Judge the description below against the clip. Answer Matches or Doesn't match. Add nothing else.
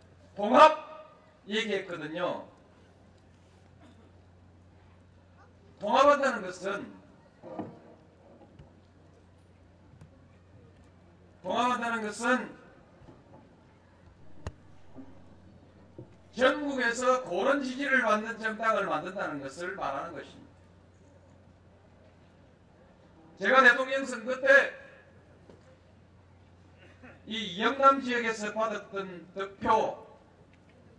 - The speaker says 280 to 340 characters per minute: Doesn't match